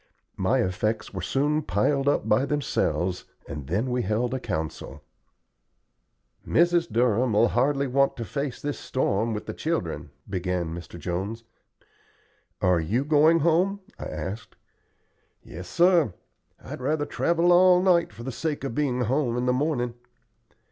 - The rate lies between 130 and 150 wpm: Yes, average, 145 wpm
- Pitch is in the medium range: No, low, 125 Hz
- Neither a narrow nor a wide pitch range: No, wide, 6.4 semitones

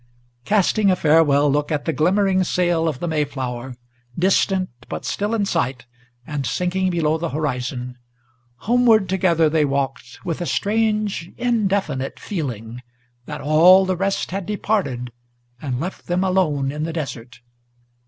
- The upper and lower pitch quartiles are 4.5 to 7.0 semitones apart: Yes, average, 5.3 semitones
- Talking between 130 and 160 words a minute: Yes, average, 145 wpm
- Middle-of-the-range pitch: Yes, medium, 165 Hz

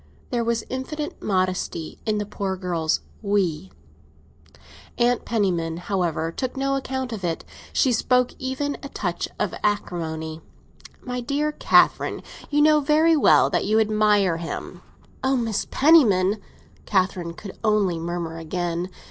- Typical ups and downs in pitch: No, wide, 6.7 semitones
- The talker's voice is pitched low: No, high, 210 Hz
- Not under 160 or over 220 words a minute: No, average, 140 wpm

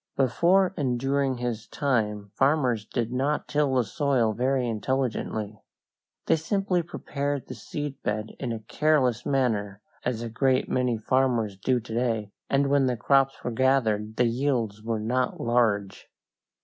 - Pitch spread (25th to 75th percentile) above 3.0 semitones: Yes, average, 3.7 semitones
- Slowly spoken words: No, average, 150 wpm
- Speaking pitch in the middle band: No, low, 125 Hz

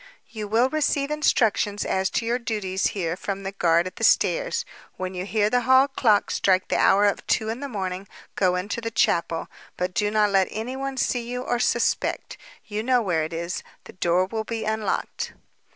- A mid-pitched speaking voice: No, high, 210 Hz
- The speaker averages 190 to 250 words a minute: Yes, average, 200 wpm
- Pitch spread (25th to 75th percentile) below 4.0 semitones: No, average, 4.5 semitones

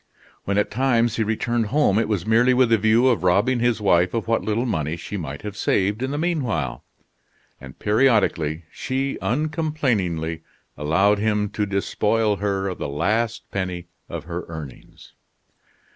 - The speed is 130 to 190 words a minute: Yes, average, 165 wpm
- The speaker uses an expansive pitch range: No, average, 4.8 semitones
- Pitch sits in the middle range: No, low, 105 Hz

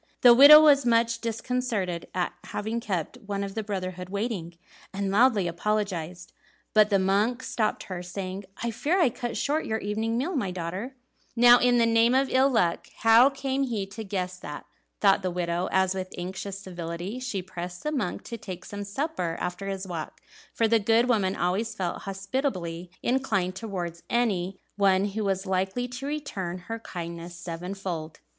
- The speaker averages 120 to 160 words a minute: No, average, 175 wpm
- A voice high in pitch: Yes, high, 200 Hz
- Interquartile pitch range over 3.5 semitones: Yes, average, 4.4 semitones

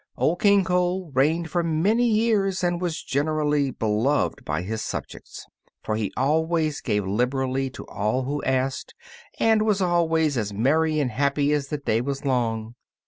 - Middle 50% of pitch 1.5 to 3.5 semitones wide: No, average, 5.1 semitones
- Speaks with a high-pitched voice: No, medium, 145 Hz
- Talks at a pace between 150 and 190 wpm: Yes, average, 160 wpm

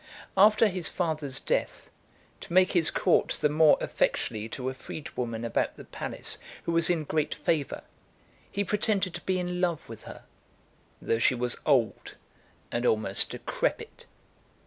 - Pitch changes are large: Yes, wide, 6.4 semitones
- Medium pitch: Yes, medium, 155 Hz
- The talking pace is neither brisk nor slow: Yes, average, 150 wpm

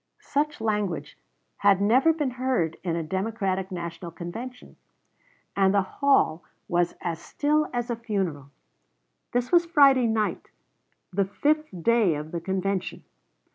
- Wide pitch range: Yes, wide, 6.3 semitones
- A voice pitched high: Yes, high, 200 Hz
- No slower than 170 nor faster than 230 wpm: No, slow, 135 wpm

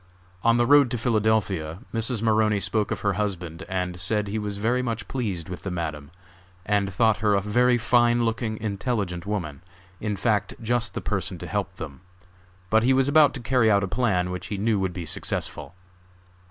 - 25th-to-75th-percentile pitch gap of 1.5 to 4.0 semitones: Yes, average, 3.7 semitones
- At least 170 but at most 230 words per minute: Yes, average, 195 wpm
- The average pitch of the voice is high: No, low, 105 Hz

